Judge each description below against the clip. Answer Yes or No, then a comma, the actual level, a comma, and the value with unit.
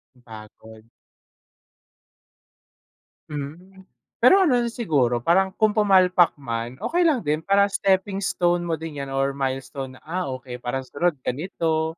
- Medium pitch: Yes, medium, 160 Hz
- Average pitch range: No, wide, 6.4 semitones